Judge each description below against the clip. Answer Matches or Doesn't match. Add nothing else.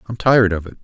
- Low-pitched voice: Matches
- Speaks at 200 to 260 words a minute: Doesn't match